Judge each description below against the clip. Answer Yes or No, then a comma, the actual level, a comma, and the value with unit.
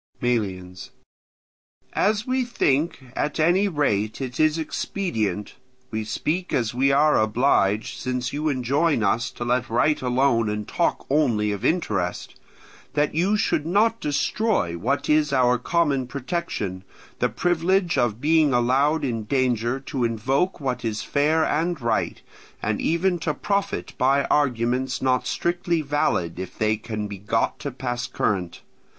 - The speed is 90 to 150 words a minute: Yes, average, 140 wpm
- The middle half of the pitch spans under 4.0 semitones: No, average, 5.3 semitones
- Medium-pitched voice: No, low, 130 Hz